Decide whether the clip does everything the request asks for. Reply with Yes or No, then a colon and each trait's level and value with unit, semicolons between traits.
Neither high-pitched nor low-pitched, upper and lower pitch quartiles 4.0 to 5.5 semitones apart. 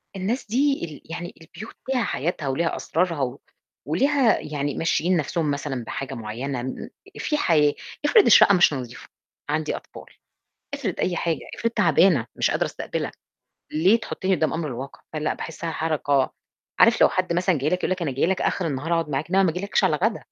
Yes: medium, 165 Hz; average, 4.5 semitones